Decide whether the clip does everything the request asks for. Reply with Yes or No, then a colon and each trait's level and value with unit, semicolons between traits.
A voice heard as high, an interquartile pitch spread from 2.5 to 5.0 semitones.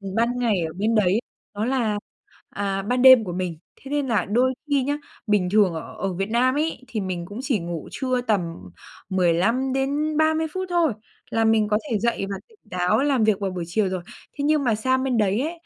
No: high, 225 Hz; wide, 5.4 semitones